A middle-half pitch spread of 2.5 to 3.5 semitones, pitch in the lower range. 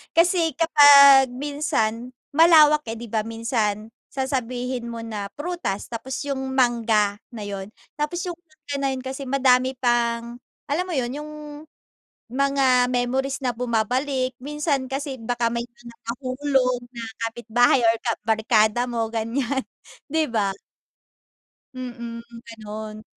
No: average, 3.2 semitones; very high, 250 Hz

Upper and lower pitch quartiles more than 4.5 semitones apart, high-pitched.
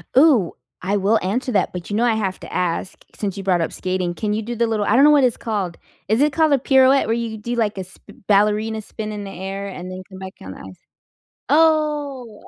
No: average, 4.2 semitones; high, 215 Hz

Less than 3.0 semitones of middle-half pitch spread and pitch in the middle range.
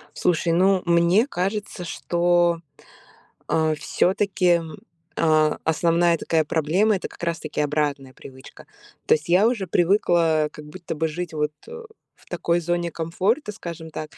Yes: narrow, 2.6 semitones; medium, 170 Hz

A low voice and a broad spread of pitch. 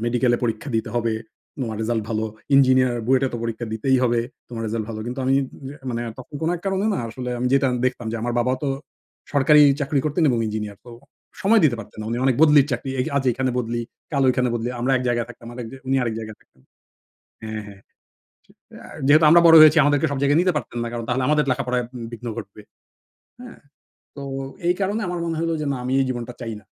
No: low, 125 Hz; average, 3.3 semitones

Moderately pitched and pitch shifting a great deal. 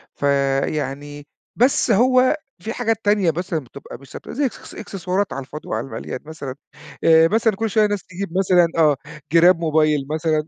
Yes: medium, 165 Hz; wide, 6.0 semitones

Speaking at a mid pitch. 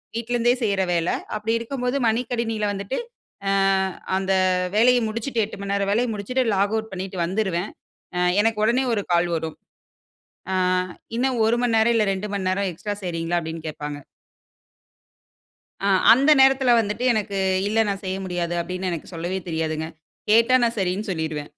No: high, 205 Hz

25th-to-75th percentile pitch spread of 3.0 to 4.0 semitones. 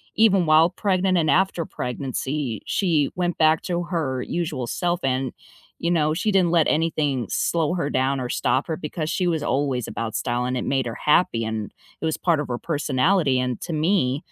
No: average, 4.9 semitones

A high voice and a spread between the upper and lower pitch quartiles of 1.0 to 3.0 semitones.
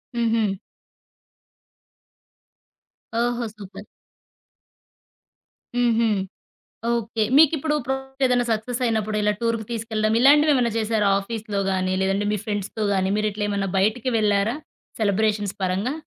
Yes: high, 220 Hz; narrow, 2.6 semitones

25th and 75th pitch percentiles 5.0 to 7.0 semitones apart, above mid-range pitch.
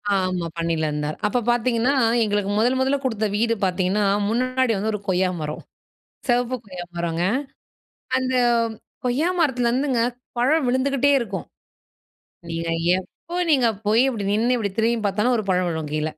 Yes: wide, 5.5 semitones; high, 225 Hz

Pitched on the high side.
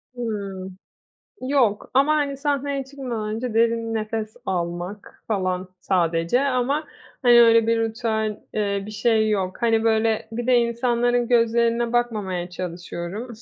Yes: high, 225 Hz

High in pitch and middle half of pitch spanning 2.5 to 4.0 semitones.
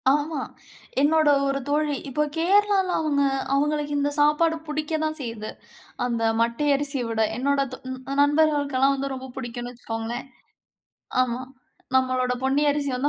Yes: very high, 280 Hz; average, 2.9 semitones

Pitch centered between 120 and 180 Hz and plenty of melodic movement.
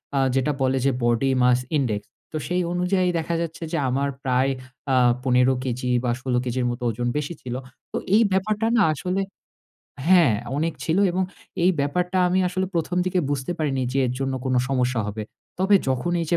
Yes: medium, 140 Hz; wide, 5.8 semitones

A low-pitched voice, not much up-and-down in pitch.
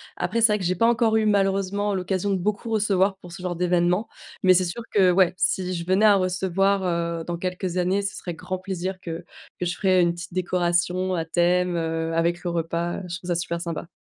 No: medium, 180 Hz; narrow, 1.9 semitones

